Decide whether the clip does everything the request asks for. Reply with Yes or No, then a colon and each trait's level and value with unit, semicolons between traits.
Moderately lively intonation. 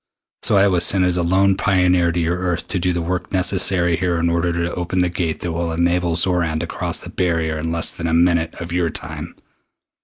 No: narrow, 1.3 semitones